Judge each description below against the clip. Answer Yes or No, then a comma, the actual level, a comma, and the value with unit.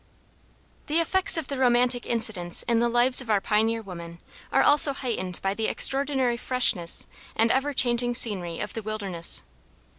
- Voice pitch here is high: Yes, high, 235 Hz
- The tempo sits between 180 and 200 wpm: No, average, 160 wpm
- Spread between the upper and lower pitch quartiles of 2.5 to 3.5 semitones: No, average, 4.1 semitones